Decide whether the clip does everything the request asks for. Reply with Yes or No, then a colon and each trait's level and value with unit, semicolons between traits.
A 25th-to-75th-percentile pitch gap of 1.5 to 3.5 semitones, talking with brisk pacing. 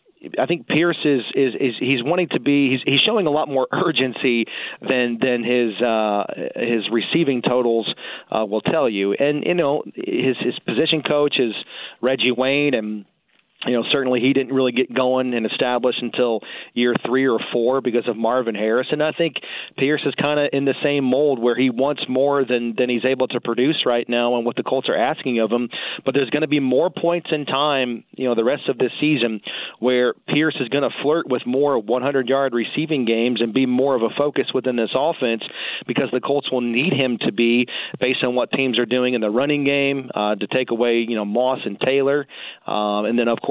Yes: average, 2.7 semitones; fast, 215 wpm